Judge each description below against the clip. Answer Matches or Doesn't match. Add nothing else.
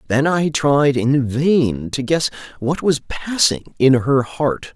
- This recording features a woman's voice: Doesn't match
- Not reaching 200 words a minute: Matches